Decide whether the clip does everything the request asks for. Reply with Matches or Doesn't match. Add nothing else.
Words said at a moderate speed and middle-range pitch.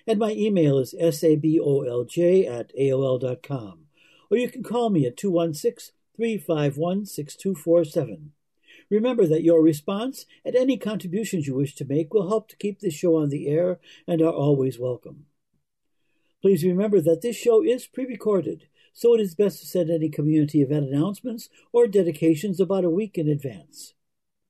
Matches